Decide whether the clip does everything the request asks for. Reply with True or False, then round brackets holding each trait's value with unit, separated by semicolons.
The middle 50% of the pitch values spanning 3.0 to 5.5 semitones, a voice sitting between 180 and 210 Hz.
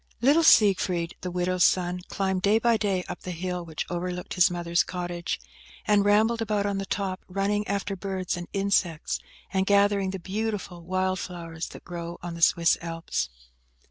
False (2.4 semitones; 185 Hz)